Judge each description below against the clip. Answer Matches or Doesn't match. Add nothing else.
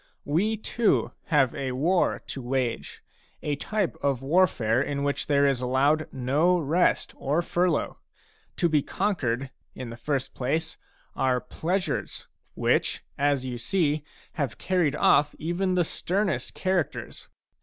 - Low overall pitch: Doesn't match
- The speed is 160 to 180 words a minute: Doesn't match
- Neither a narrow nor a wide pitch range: Matches